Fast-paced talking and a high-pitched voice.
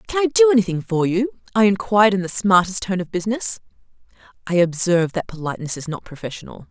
No: average, 190 wpm; high, 195 Hz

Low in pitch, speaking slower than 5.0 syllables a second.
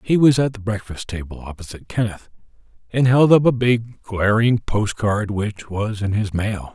Yes: low, 110 Hz; 4.6 syllables/s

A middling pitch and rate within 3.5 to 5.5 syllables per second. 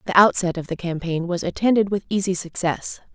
No: medium, 180 Hz; 5.7 syllables/s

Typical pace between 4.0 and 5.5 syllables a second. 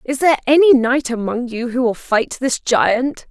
Yes: 4.5 syllables/s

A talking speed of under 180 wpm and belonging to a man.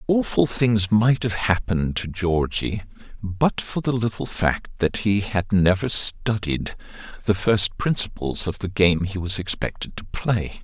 Yes: average, 160 wpm; male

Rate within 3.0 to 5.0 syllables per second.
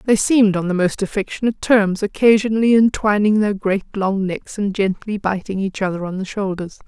No: 5.4 syllables/s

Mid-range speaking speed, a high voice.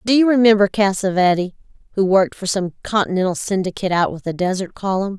Yes: average, 175 wpm; high, 195 Hz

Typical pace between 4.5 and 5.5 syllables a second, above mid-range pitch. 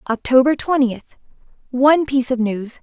Yes: 5.2 syllables/s; very high, 260 Hz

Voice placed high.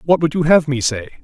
No: medium, 150 Hz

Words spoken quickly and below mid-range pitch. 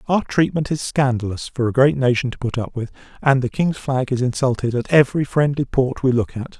Yes: fast, 225 wpm; low, 130 Hz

